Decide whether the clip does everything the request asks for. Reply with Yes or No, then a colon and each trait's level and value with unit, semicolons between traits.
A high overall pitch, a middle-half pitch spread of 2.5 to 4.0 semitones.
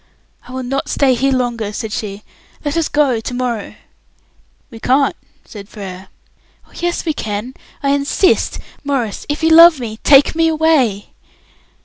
No: very high, 255 Hz; average, 4.9 semitones